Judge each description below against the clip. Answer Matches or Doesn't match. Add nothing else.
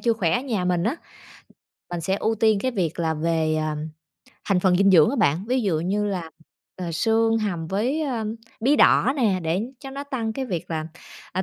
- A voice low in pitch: Doesn't match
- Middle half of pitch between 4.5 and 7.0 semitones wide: Matches